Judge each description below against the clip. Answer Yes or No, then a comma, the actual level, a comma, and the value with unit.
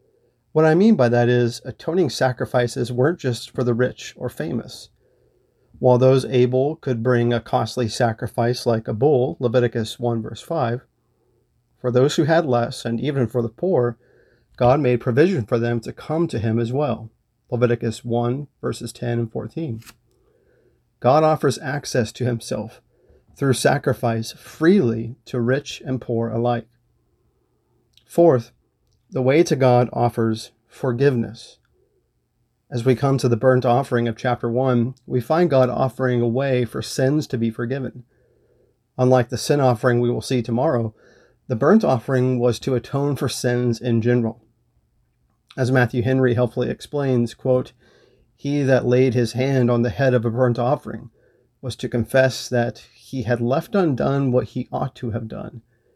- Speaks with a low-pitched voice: Yes, low, 125 Hz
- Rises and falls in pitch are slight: Yes, narrow, 1.8 semitones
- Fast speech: No, average, 160 wpm